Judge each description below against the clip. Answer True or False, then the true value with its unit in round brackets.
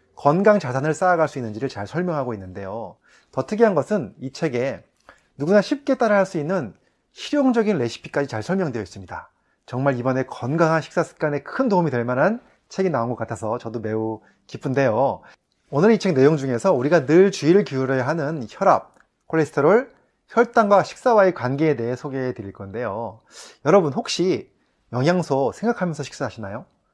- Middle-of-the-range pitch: True (155 Hz)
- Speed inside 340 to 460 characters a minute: True (365 characters per minute)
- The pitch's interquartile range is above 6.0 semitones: True (7.3 semitones)